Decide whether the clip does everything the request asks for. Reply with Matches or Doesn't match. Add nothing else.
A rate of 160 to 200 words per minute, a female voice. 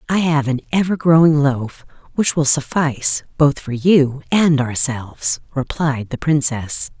Doesn't match